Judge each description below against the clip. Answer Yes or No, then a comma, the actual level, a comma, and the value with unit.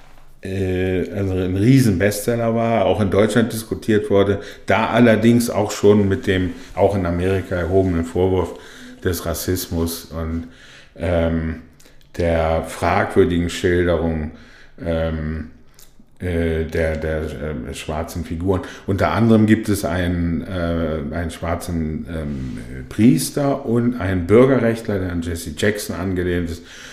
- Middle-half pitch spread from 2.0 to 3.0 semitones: No, average, 3.6 semitones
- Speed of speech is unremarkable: No, slow, 120 wpm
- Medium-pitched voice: No, very low, 90 Hz